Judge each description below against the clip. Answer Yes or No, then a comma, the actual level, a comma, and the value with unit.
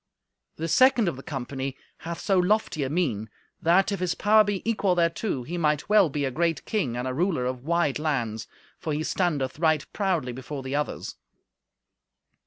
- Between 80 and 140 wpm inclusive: No, average, 185 wpm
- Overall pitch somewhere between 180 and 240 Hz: No, medium, 160 Hz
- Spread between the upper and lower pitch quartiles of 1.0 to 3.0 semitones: No, wide, 5.5 semitones